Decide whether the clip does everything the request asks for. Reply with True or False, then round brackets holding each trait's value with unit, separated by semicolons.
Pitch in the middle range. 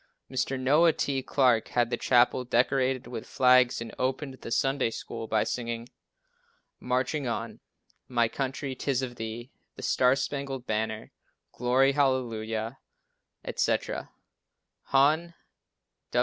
False (130 Hz)